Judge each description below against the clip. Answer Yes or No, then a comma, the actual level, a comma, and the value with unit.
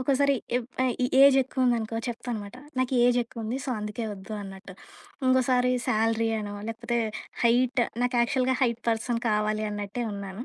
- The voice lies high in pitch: Yes, high, 235 Hz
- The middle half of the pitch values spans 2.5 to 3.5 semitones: Yes, average, 2.8 semitones